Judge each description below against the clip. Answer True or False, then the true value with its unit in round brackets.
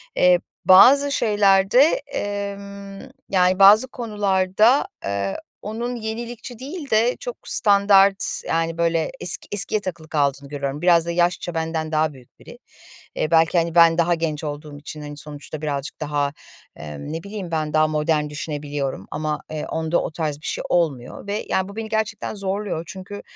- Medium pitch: True (170 Hz)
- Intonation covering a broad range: False (4.9 semitones)